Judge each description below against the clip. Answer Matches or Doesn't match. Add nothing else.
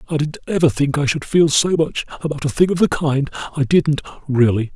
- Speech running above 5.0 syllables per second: Matches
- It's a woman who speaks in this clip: Doesn't match